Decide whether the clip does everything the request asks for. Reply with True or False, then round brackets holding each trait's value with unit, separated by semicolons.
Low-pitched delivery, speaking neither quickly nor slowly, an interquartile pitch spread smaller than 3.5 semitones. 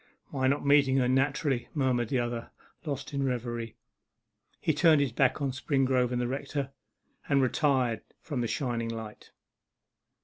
True (130 Hz; 150 wpm; 2.5 semitones)